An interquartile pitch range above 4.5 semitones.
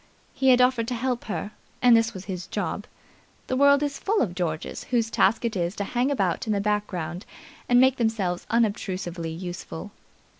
Yes: average, 5.2 semitones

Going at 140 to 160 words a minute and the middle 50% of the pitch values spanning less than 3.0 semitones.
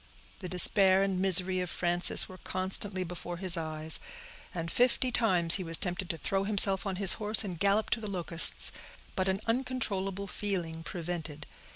No: average, 170 wpm; narrow, 2.4 semitones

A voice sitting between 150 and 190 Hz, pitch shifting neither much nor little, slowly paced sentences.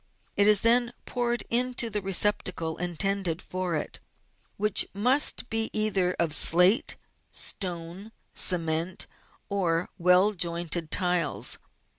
Yes: medium, 185 Hz; average, 3.7 semitones; slow, 115 wpm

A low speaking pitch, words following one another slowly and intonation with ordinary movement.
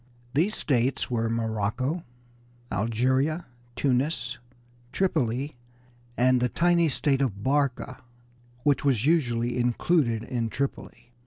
Yes: low, 130 Hz; slow, 100 wpm; average, 3.6 semitones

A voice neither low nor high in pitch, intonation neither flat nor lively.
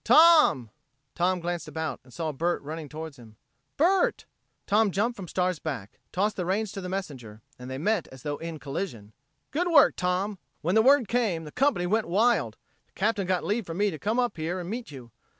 No: medium, 180 Hz; wide, 5.8 semitones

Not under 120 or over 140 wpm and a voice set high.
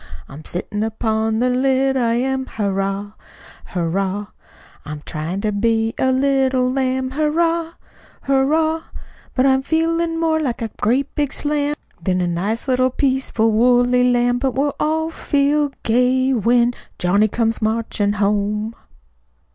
Yes: slow, 135 wpm; very high, 250 Hz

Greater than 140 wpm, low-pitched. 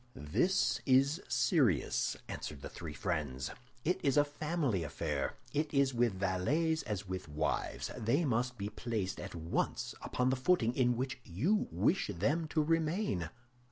Yes: average, 155 wpm; low, 125 Hz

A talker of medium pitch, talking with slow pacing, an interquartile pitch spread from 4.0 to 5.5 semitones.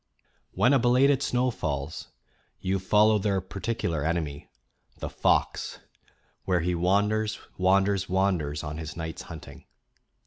No: very low, 95 Hz; slow, 125 wpm; average, 4.7 semitones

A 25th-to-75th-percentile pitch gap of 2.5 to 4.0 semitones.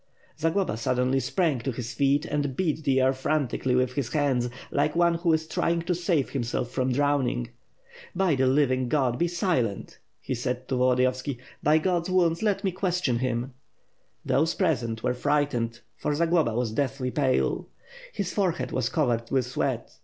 No: average, 4.7 semitones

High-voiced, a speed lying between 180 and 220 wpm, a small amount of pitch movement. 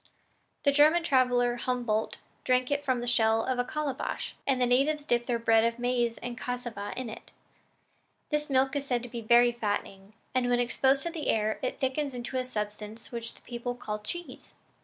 Yes: high, 245 Hz; average, 195 wpm; narrow, 2.3 semitones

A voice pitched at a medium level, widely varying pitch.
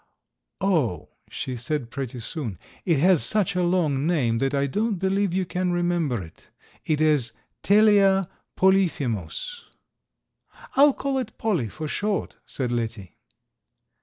Yes: medium, 165 Hz; wide, 7.0 semitones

